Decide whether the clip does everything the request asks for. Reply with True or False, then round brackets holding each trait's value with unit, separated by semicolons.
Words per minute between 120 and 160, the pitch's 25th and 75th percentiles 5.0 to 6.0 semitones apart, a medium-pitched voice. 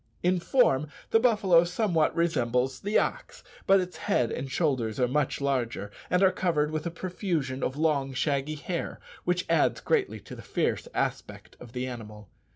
False (170 wpm; 5.6 semitones; 155 Hz)